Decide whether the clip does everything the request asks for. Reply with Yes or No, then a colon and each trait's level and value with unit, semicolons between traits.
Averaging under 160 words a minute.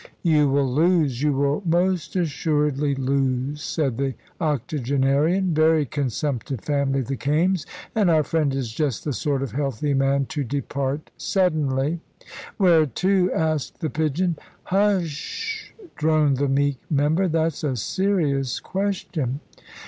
Yes: average, 140 wpm